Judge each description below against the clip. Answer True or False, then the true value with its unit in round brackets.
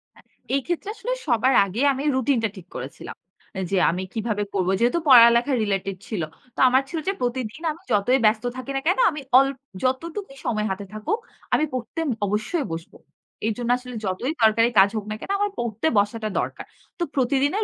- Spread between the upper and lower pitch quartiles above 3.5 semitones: True (4.7 semitones)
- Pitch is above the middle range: True (240 Hz)